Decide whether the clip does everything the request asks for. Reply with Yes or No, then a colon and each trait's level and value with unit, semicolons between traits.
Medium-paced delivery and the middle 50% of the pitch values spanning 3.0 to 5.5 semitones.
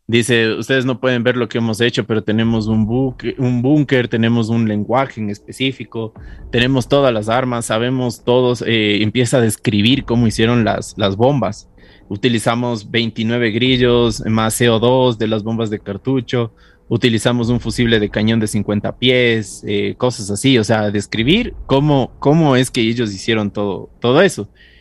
No: average, 165 wpm; narrow, 2.5 semitones